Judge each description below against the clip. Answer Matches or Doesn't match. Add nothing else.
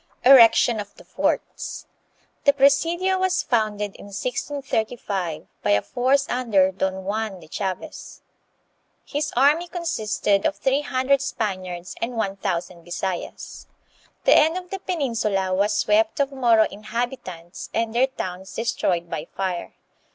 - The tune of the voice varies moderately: Doesn't match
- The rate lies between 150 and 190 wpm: Doesn't match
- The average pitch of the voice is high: Matches